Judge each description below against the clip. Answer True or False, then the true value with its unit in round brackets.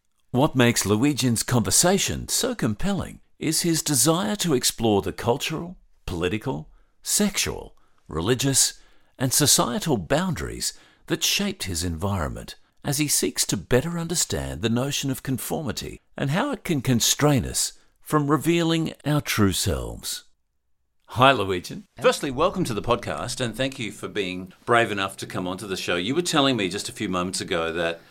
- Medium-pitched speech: False (125 Hz)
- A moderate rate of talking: True (155 wpm)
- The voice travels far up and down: True (7.6 semitones)